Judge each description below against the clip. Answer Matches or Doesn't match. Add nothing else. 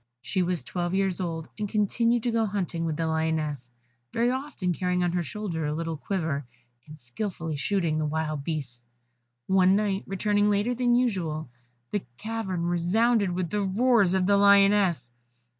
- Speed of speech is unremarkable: Matches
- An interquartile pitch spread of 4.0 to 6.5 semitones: Matches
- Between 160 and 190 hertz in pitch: Matches